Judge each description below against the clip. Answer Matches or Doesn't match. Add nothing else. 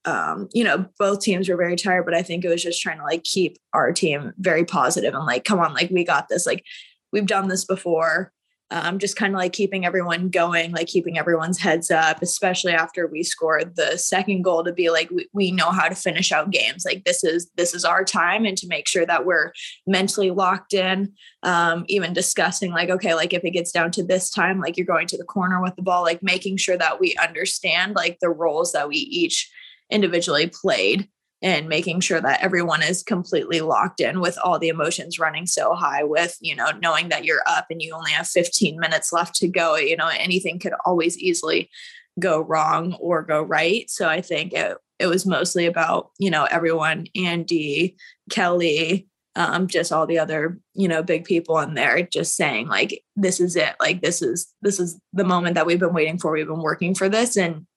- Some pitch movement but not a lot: Doesn't match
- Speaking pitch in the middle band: Matches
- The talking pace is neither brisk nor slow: Doesn't match